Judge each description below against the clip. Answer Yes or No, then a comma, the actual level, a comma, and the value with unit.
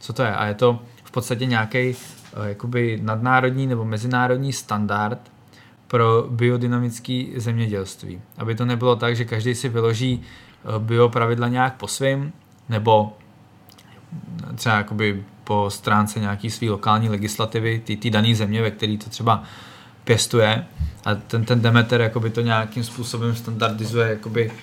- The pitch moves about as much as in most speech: No, narrow, 2.2 semitones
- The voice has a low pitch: Yes, low, 115 Hz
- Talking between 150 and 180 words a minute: No, average, 135 wpm